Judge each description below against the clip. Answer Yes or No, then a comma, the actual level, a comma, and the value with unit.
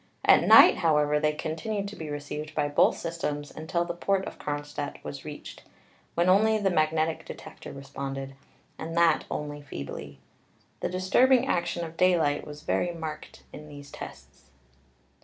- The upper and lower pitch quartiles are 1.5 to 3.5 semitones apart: Yes, average, 2.8 semitones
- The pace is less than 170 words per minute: Yes, average, 155 wpm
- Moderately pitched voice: Yes, medium, 155 Hz